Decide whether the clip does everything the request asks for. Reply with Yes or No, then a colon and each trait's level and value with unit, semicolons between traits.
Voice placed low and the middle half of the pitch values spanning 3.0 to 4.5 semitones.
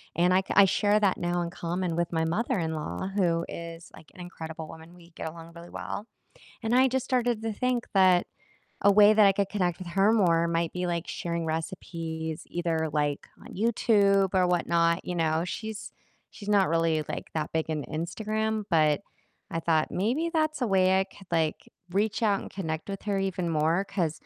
No: medium, 180 Hz; average, 3.6 semitones